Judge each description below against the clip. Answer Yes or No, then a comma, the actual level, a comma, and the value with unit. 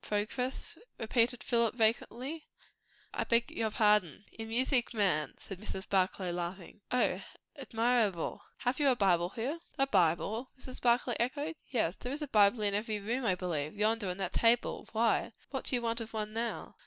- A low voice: No, high, 225 Hz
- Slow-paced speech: No, average, 175 wpm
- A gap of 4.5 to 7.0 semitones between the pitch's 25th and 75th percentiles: No, average, 3.6 semitones